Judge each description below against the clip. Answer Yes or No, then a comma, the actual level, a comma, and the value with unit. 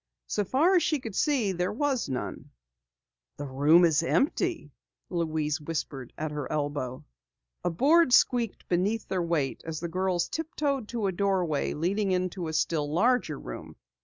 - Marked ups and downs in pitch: Yes, wide, 7.0 semitones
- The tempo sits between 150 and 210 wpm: Yes, average, 160 wpm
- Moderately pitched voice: Yes, medium, 180 Hz